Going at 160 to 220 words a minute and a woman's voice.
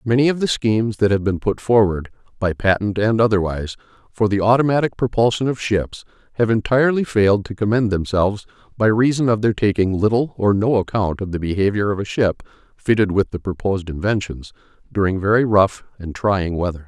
No: average, 180 wpm; male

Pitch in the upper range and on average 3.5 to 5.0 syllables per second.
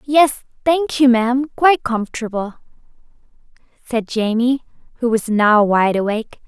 Yes: high, 240 Hz; 4.8 syllables/s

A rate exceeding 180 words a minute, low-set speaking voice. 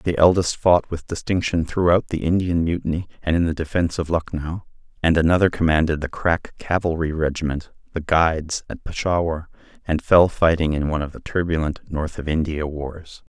No: average, 170 wpm; very low, 80 Hz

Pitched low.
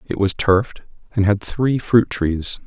Yes: low, 105 Hz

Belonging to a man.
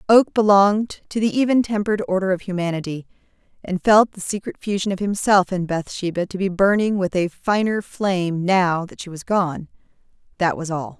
No: female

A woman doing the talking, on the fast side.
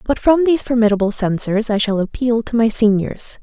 No: female; average, 195 wpm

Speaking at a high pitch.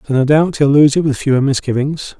No: medium, 140 Hz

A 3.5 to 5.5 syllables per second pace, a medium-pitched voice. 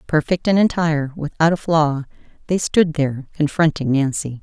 Yes: 5.0 syllables/s; medium, 155 Hz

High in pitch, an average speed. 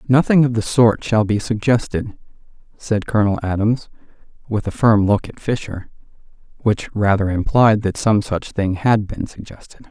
No: low, 110 Hz; average, 155 wpm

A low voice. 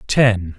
Yes: low, 105 Hz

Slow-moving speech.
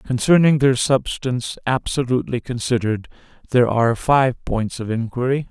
Yes: slow, 120 wpm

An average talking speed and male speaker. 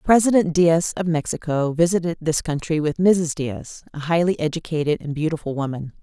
No: average, 160 wpm; female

